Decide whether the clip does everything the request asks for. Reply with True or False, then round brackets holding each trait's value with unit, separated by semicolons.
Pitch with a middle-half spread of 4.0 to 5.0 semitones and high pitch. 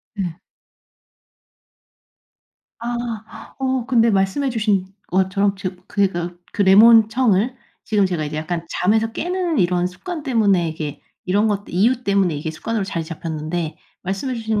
True (4.5 semitones; 200 Hz)